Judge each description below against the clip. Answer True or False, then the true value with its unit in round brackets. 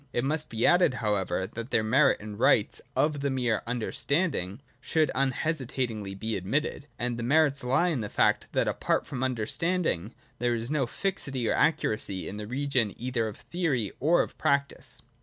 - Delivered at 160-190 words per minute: True (175 wpm)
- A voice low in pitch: True (125 Hz)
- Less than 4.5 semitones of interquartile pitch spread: False (4.8 semitones)